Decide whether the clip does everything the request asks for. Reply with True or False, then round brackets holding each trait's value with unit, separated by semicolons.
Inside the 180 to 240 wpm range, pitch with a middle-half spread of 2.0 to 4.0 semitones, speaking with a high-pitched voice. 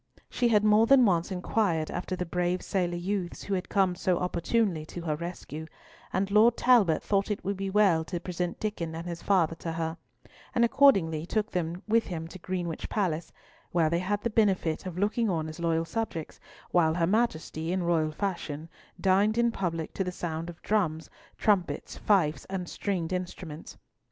False (185 wpm; 3.6 semitones; 180 Hz)